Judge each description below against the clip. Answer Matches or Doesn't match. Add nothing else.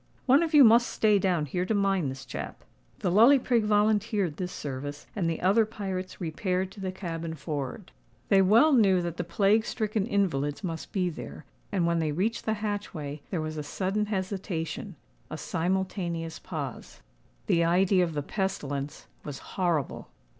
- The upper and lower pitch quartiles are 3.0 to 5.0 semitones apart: Matches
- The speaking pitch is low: Doesn't match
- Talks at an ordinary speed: Matches